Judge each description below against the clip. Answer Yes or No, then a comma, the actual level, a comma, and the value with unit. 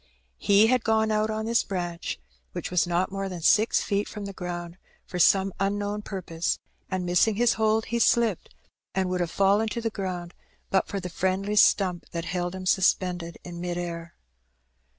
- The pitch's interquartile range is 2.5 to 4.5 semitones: Yes, average, 3.0 semitones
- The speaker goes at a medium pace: Yes, average, 190 wpm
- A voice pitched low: No, high, 190 Hz